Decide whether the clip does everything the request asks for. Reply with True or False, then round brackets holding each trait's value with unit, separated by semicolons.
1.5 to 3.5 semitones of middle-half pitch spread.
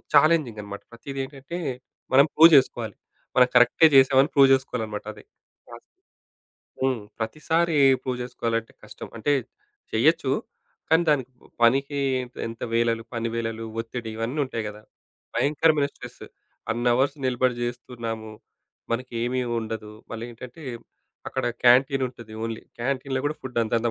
True (3.1 semitones)